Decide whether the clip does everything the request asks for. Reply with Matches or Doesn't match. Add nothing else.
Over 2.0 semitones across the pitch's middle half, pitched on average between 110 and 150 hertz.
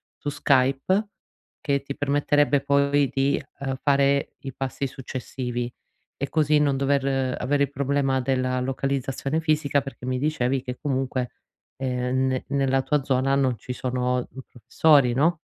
Doesn't match